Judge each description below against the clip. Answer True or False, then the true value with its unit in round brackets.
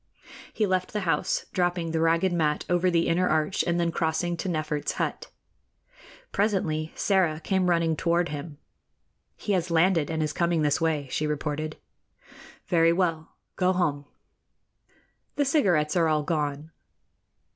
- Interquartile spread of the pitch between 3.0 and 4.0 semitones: False (2.5 semitones)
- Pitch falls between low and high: True (165 Hz)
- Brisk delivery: False (145 wpm)